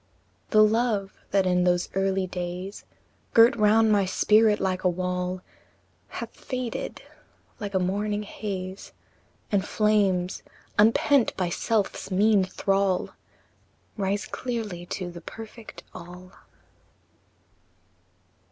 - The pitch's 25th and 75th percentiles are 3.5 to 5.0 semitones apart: No, average, 2.7 semitones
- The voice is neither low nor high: No, high, 195 Hz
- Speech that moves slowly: Yes, slow, 110 wpm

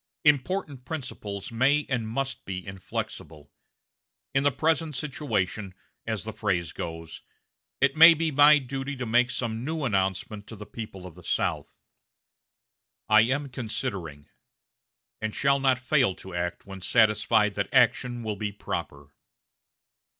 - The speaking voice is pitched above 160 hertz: No, low, 115 Hz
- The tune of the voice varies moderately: No, wide, 5.9 semitones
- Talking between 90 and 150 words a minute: Yes, average, 140 wpm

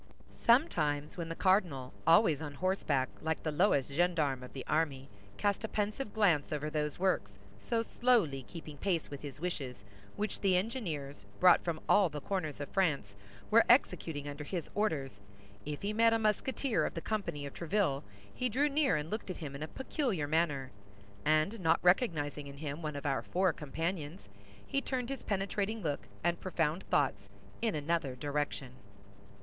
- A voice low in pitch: No, medium, 160 Hz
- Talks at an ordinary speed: Yes, average, 175 wpm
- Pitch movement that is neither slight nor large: No, wide, 5.8 semitones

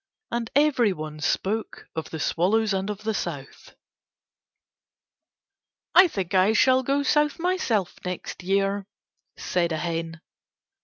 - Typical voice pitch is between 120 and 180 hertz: No, high, 195 Hz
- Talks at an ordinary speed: No, slow, 115 wpm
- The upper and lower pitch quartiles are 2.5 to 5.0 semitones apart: No, wide, 5.6 semitones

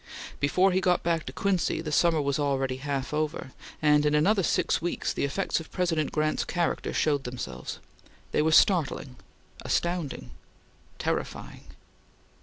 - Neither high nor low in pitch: Yes, medium, 155 Hz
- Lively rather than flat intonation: No, average, 3.5 semitones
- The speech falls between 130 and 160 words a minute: Yes, average, 145 wpm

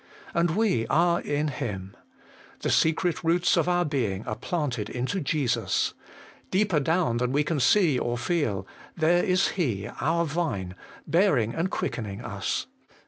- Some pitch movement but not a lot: No, wide, 6.8 semitones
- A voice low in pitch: No, medium, 150 Hz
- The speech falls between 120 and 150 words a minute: Yes, average, 145 wpm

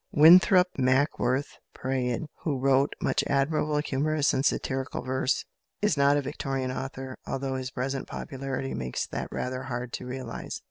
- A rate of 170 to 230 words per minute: No, average, 145 wpm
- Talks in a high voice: No, low, 135 Hz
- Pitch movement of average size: No, narrow, 1.9 semitones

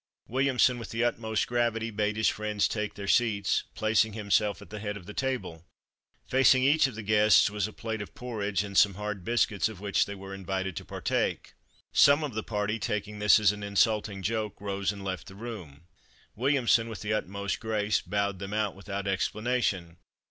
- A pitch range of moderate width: No, narrow, 2.2 semitones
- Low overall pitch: Yes, low, 105 Hz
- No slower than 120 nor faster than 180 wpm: No, average, 190 wpm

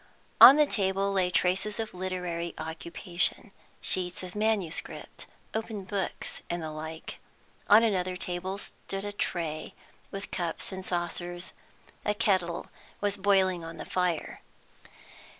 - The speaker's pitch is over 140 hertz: Yes, medium, 185 Hz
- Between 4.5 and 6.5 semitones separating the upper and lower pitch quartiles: No, narrow, 2.5 semitones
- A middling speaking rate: No, slow, 130 wpm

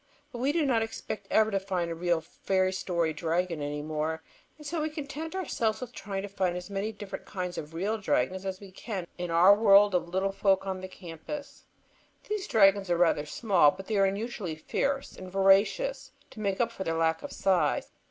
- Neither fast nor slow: No, fast, 210 wpm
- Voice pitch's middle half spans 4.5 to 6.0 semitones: No, average, 4.0 semitones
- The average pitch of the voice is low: No, high, 195 Hz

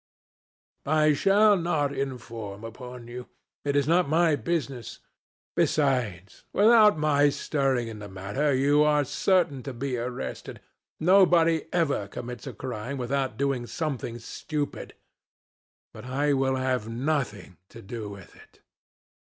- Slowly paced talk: Yes, slow, 130 wpm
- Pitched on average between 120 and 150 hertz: Yes, low, 135 Hz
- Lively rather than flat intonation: No, average, 4.2 semitones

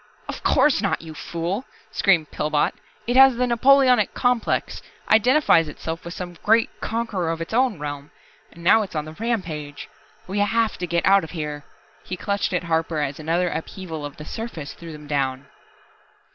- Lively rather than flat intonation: Yes, wide, 6.2 semitones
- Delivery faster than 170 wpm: Yes, average, 180 wpm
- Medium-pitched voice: Yes, medium, 175 Hz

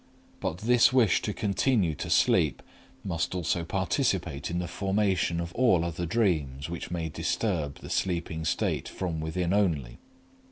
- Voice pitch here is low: Yes, very low, 85 Hz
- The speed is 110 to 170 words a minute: Yes, average, 150 wpm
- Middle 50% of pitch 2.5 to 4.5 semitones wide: Yes, average, 3.3 semitones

